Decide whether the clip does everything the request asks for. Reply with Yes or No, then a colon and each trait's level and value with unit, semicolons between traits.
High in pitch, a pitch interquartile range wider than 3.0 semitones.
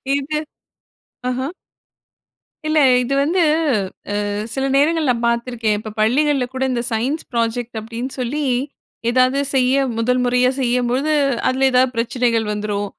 No: very high, 250 Hz; narrow, 2.5 semitones